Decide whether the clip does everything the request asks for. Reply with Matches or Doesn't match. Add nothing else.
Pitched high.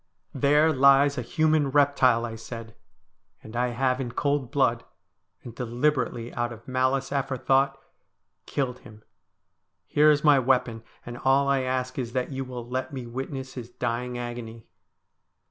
Doesn't match